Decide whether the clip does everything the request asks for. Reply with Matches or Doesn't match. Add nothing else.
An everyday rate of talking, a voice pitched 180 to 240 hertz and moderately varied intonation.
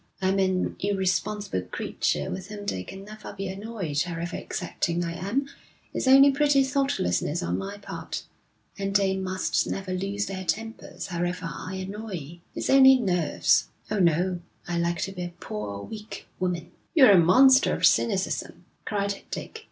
Matches